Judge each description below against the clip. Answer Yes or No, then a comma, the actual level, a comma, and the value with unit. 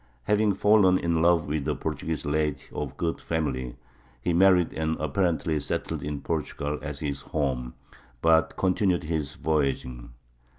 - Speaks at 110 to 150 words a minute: Yes, average, 140 wpm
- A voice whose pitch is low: Yes, very low, 80 Hz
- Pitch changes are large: No, average, 3.0 semitones